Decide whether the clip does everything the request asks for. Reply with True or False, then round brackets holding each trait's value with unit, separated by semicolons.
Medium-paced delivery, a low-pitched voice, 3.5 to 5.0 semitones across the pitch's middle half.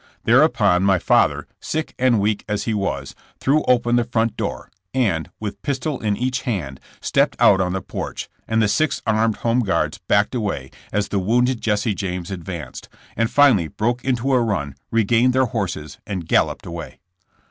True (180 wpm; 110 Hz; 4.2 semitones)